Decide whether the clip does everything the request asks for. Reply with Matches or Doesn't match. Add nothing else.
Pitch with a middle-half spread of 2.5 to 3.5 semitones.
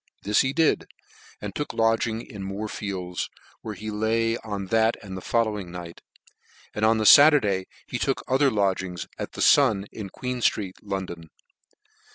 Matches